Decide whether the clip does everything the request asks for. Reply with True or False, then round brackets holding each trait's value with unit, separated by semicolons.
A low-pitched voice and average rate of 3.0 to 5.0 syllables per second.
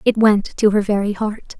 False (210 Hz; 4.7 syllables/s)